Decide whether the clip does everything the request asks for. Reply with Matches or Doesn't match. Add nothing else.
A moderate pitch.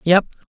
Matches